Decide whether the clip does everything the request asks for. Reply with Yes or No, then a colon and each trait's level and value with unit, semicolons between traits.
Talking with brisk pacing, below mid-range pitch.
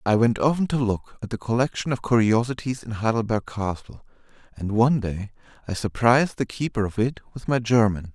No: average, 185 wpm; low, 115 Hz